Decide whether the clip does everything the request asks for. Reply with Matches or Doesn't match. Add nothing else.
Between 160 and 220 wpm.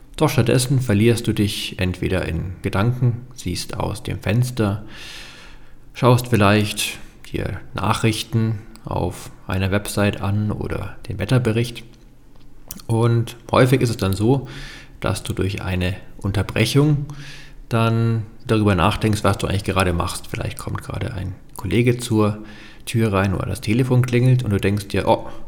Doesn't match